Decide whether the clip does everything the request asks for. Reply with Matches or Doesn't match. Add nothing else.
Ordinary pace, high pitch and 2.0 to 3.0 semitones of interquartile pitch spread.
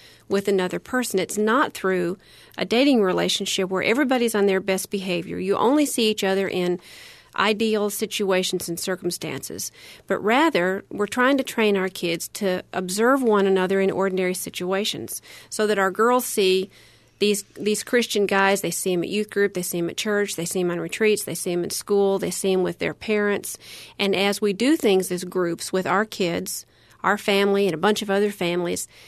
Matches